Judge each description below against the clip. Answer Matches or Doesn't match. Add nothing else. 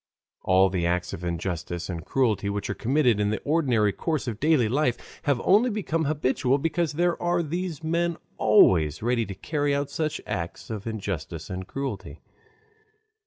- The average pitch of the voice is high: Doesn't match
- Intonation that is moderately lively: Doesn't match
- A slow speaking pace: Doesn't match